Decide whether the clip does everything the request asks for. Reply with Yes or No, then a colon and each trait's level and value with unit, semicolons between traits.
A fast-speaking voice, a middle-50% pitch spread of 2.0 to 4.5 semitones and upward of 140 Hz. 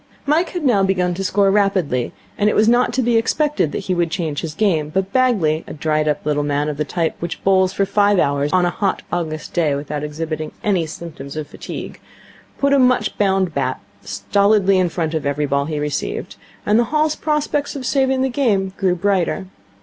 No: fast, 210 wpm; wide, 5.6 semitones; medium, 185 Hz